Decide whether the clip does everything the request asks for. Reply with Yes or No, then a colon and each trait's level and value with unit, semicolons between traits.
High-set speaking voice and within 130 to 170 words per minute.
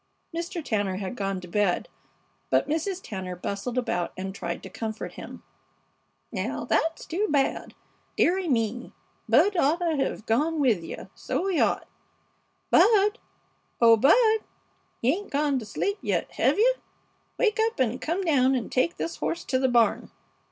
Yes: very high, 270 Hz; average, 155 wpm